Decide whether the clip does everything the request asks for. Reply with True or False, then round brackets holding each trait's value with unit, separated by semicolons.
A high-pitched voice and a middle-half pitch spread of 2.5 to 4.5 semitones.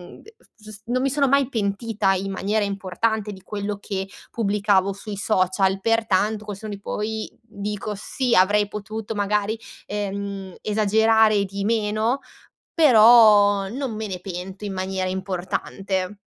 False (205 Hz; 2.0 semitones)